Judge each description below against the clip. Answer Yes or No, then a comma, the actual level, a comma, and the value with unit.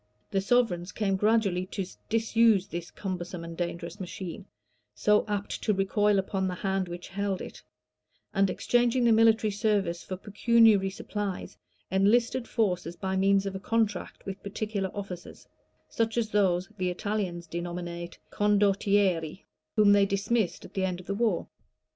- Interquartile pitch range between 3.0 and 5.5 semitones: No, narrow, 2.6 semitones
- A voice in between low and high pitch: No, high, 195 Hz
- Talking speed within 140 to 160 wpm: Yes, average, 150 wpm